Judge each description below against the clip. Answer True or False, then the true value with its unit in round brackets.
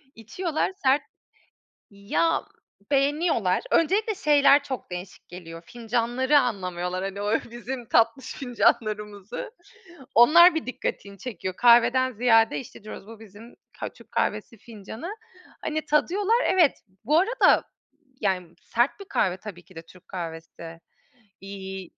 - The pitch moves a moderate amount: False (6.7 semitones)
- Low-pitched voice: False (230 Hz)